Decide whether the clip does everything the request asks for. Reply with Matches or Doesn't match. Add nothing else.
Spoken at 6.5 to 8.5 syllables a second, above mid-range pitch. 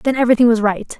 Matches